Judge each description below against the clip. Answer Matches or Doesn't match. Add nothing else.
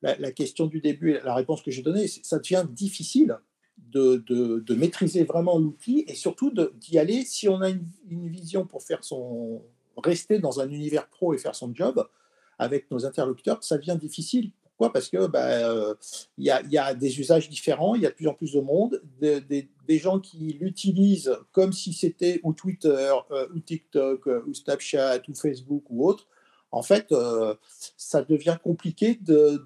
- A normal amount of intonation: Matches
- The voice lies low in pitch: Doesn't match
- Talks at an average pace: Matches